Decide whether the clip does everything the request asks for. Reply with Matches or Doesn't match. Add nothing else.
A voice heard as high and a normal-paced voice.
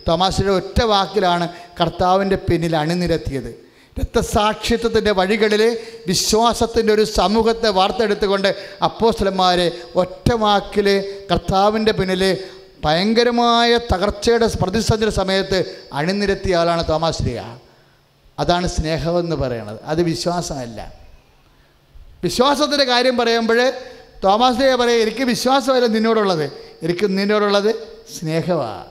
Doesn't match